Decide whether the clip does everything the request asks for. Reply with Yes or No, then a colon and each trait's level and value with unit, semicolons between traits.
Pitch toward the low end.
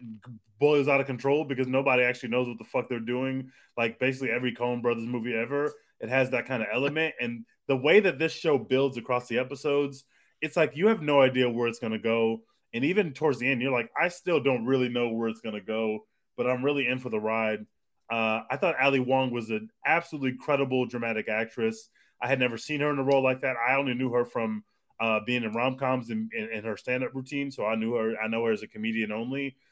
Yes: low, 125 Hz